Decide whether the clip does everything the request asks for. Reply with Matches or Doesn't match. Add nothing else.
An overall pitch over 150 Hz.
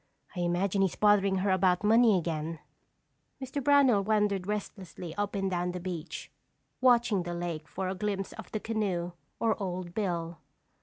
Matches